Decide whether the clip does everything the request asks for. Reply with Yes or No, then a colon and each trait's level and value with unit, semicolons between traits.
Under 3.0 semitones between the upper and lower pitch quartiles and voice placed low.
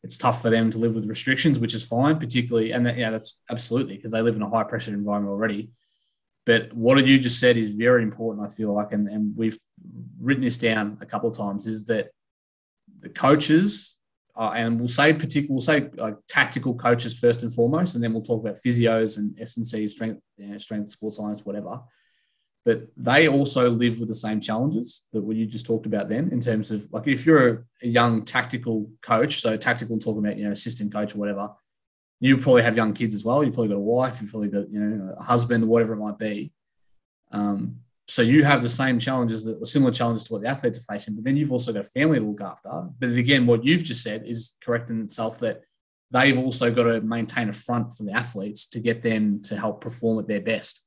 Yes: narrow, 2.4 semitones; low, 115 Hz